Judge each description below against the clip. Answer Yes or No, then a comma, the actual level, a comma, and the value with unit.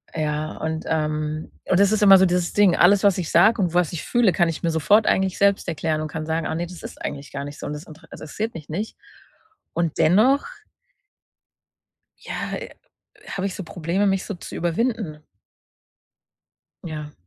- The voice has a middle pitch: Yes, medium, 170 Hz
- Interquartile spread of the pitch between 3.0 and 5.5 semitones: Yes, average, 4.0 semitones